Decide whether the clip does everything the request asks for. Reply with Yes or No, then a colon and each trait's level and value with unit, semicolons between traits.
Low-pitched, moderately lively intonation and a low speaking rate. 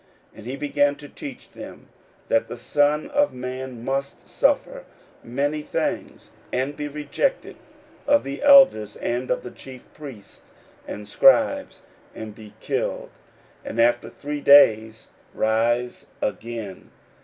Yes: low, 130 Hz; average, 4.2 semitones; slow, 130 wpm